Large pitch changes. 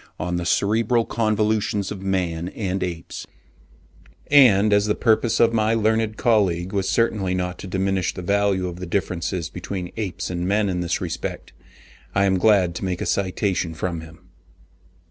No: average, 3.1 semitones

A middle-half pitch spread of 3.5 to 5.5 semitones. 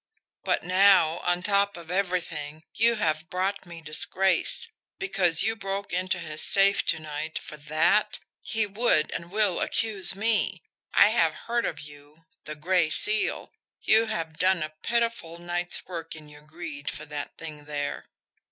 Yes: average, 4.3 semitones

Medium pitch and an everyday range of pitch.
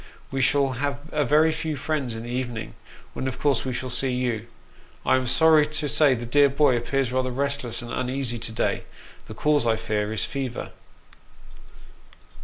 No: low, 130 Hz; average, 3.2 semitones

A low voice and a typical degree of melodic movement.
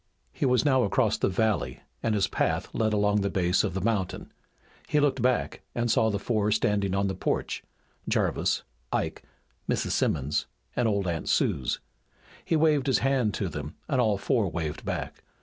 Yes: low, 105 Hz; average, 4.5 semitones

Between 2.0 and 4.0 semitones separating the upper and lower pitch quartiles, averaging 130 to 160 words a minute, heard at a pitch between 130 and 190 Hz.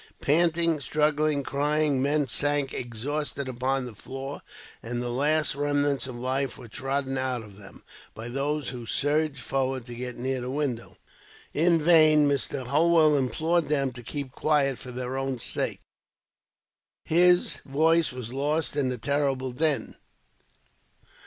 Yes: average, 2.8 semitones; average, 145 wpm; medium, 140 Hz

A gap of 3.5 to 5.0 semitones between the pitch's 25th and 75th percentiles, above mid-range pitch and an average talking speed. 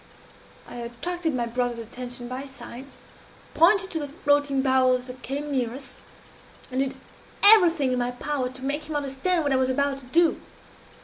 No: average, 2.7 semitones; very high, 270 Hz; average, 175 wpm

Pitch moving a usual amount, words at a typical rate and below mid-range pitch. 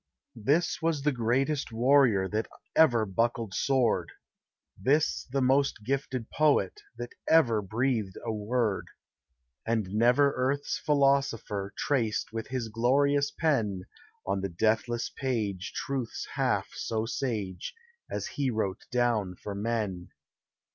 No: average, 4.3 semitones; slow, 120 wpm; low, 120 Hz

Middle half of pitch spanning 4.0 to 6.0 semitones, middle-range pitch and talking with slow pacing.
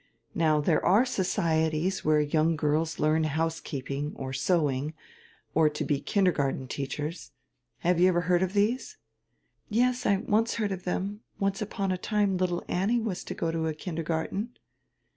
No: average, 4.3 semitones; medium, 170 Hz; average, 160 wpm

